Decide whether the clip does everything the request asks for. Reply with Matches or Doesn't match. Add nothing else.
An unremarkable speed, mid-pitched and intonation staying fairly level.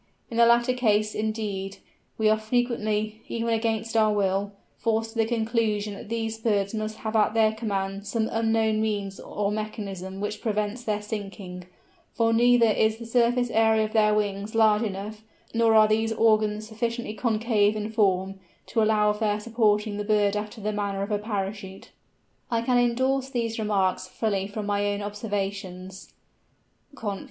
Doesn't match